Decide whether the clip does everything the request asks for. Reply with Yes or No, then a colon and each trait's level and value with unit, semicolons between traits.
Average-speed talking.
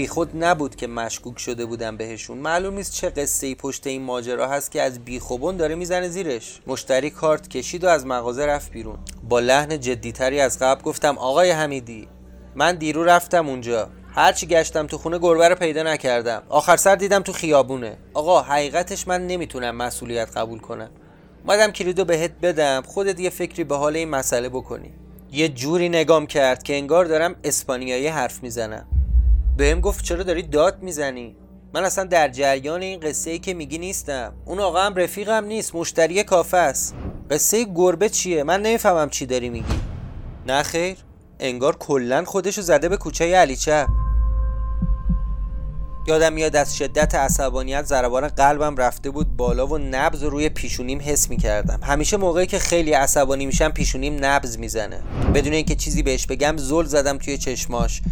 No: fast, 165 wpm